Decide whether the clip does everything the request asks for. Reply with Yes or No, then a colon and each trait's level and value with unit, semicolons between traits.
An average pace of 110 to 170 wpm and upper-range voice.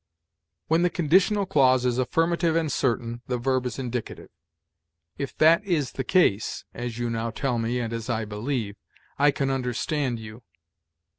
No: average, 160 wpm; low, 130 Hz